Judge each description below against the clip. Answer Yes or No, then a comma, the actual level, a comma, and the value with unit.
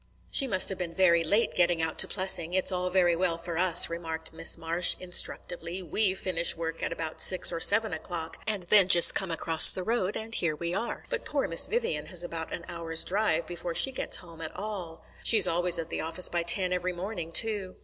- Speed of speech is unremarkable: No, fast, 220 wpm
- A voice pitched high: No, medium, 175 Hz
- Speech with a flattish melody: Yes, narrow, 2.3 semitones